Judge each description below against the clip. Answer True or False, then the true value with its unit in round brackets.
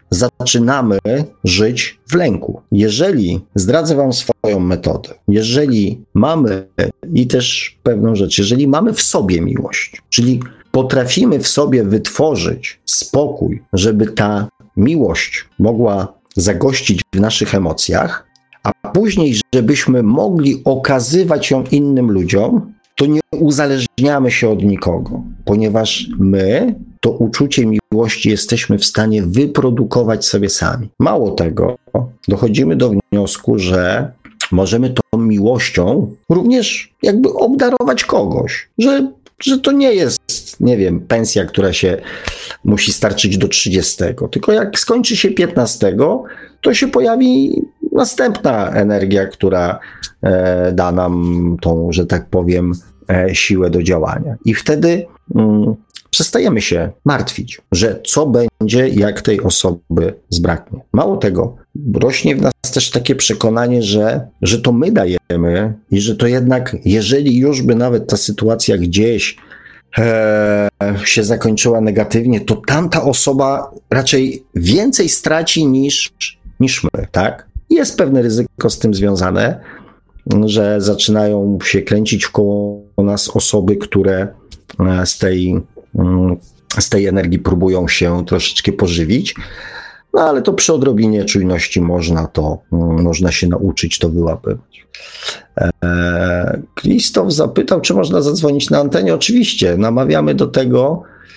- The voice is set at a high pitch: False (110 Hz)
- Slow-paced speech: False (120 wpm)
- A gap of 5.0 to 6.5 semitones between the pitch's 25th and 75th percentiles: True (5.4 semitones)